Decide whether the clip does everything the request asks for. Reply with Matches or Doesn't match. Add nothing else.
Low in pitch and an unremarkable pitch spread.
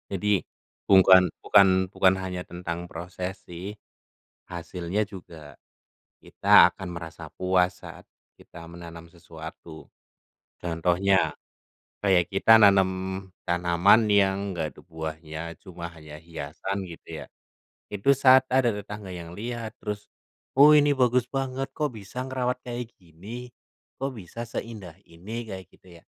Matches